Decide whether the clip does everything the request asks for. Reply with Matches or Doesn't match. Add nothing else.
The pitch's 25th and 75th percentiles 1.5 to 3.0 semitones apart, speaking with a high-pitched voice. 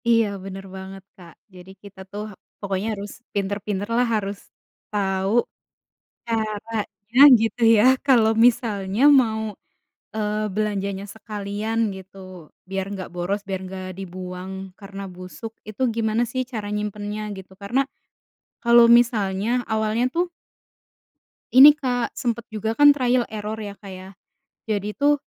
Matches